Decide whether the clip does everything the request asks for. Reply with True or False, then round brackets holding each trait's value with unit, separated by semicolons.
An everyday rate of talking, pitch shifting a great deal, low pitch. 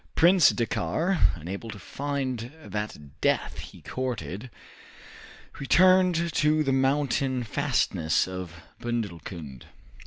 False (95 wpm; 7.6 semitones; 125 Hz)